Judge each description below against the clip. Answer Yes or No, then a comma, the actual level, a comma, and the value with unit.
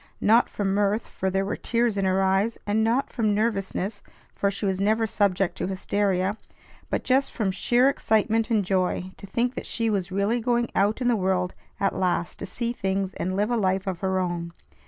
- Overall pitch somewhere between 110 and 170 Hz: No, high, 200 Hz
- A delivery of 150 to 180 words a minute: No, fast, 205 wpm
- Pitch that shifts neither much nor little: Yes, average, 3.0 semitones